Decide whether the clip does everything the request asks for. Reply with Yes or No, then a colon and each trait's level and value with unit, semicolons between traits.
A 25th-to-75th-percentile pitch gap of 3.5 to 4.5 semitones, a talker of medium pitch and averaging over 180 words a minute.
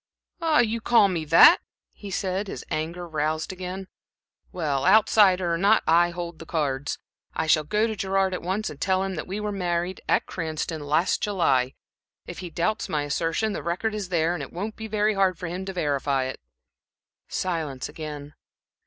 Yes: average, 3.9 semitones; medium, 175 Hz; average, 190 wpm